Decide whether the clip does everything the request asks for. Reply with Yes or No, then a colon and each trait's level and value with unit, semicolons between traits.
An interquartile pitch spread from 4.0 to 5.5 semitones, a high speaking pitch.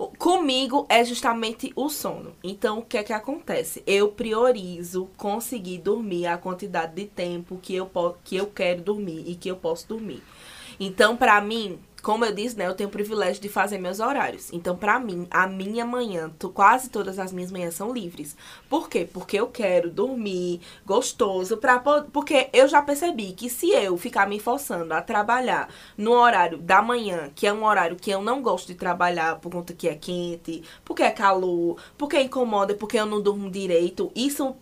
Yes: average, 5.0 semitones; high, 205 Hz